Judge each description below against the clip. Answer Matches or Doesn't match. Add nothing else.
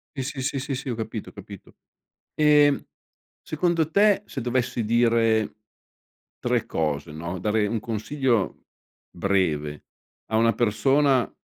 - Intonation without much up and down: Doesn't match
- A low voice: Matches